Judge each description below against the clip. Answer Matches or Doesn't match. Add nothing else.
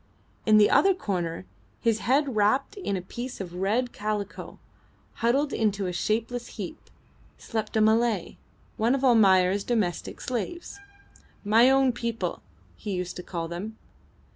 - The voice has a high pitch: Matches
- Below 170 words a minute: Matches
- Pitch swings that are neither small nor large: Matches